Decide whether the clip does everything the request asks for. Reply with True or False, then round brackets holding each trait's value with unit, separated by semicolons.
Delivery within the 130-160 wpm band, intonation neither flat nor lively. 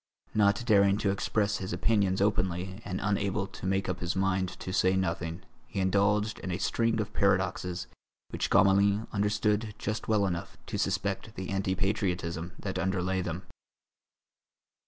False (155 wpm; 1.8 semitones)